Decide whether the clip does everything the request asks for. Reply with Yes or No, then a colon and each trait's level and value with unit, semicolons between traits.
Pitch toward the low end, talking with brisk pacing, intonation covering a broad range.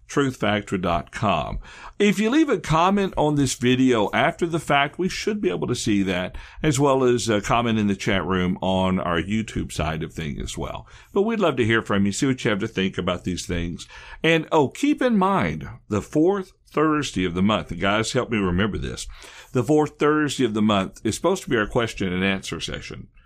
Yes: low, 115 Hz; fast, 215 wpm; wide, 8.2 semitones